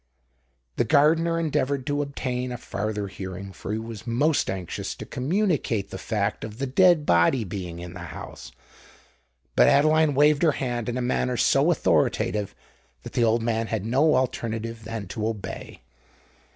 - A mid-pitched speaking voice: No, low, 120 Hz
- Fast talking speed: No, average, 165 wpm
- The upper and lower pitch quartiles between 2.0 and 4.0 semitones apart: No, average, 5.1 semitones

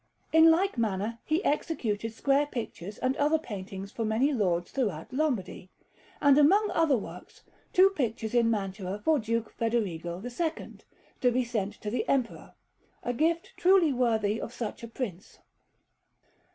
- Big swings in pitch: Yes, wide, 5.8 semitones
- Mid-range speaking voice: No, high, 235 Hz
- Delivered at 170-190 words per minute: No, average, 150 wpm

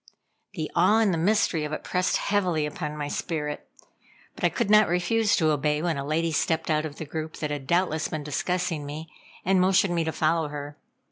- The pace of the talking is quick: Yes, fast, 210 wpm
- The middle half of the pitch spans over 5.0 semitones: No, average, 3.2 semitones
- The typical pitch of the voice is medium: Yes, medium, 160 Hz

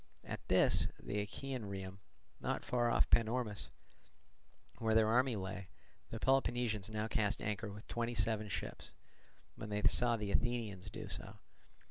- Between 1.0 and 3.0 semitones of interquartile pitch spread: Yes, narrow, 2.6 semitones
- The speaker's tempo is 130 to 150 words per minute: Yes, average, 145 wpm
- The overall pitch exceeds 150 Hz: No, low, 110 Hz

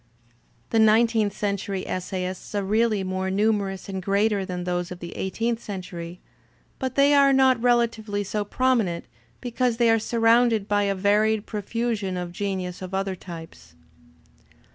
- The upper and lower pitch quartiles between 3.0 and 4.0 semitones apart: Yes, average, 3.4 semitones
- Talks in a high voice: Yes, high, 205 Hz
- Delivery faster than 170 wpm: No, average, 155 wpm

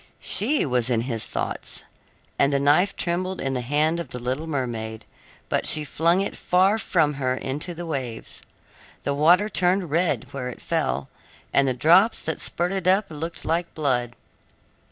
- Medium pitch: Yes, medium, 150 Hz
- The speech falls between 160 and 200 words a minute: Yes, average, 170 wpm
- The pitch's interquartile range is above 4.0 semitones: Yes, wide, 5.5 semitones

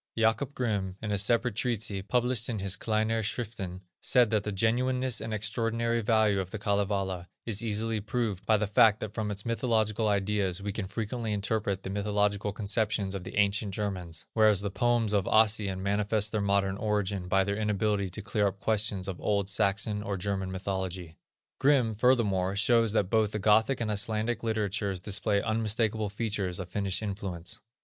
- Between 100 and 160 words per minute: No, average, 175 wpm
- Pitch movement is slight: Yes, narrow, 2.1 semitones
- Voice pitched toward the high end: No, low, 105 Hz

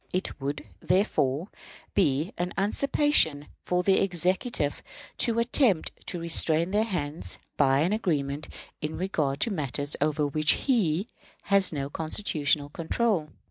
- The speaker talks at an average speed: No, slow, 130 wpm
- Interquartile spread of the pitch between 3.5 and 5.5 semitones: Yes, average, 5.2 semitones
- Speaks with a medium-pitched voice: Yes, medium, 165 Hz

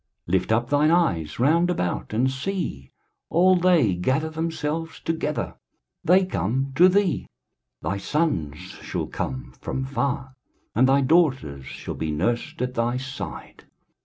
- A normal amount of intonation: No, wide, 8.8 semitones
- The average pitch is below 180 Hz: Yes, low, 135 Hz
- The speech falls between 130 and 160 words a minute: Yes, average, 140 wpm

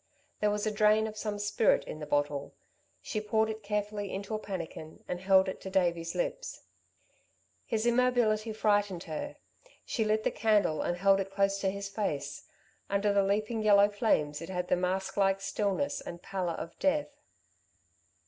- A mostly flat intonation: Yes, narrow, 2.3 semitones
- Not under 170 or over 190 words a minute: Yes, average, 175 wpm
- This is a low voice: No, high, 200 Hz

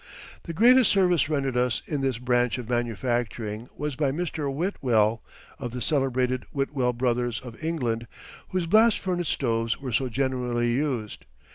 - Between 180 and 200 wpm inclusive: No, average, 150 wpm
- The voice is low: Yes, low, 130 Hz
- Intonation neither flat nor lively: Yes, average, 3.9 semitones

